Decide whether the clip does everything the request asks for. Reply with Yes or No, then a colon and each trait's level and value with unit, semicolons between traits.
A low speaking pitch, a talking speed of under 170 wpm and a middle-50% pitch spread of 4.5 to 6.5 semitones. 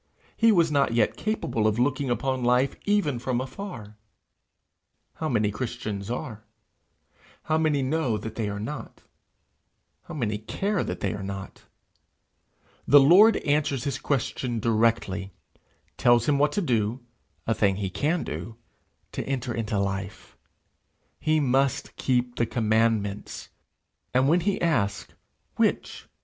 Yes: low, 125 Hz; slow, 135 wpm; average, 5.2 semitones